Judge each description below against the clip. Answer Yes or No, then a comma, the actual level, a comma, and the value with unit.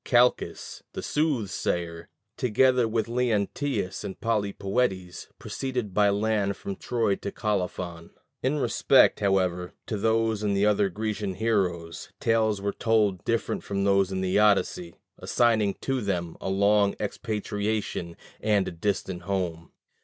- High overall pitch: No, low, 100 Hz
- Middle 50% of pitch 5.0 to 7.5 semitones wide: No, average, 2.9 semitones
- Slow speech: Yes, slow, 130 wpm